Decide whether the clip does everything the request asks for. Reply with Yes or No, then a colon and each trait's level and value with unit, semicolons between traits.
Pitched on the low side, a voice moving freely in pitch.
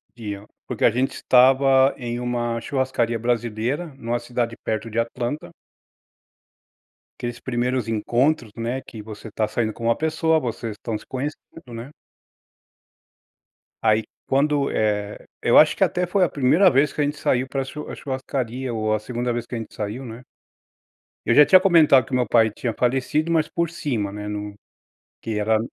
No: low, 120 Hz; average, 3.3 semitones